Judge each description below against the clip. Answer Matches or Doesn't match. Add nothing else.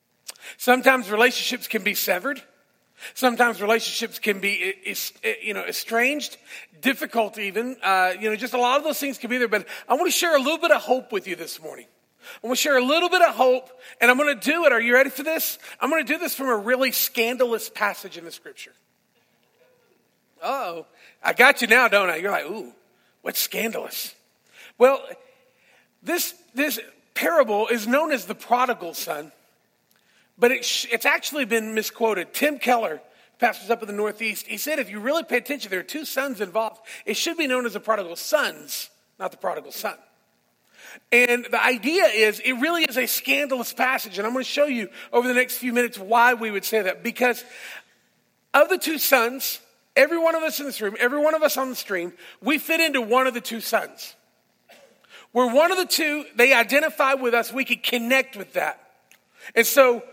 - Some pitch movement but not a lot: Matches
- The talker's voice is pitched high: Matches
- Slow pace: Doesn't match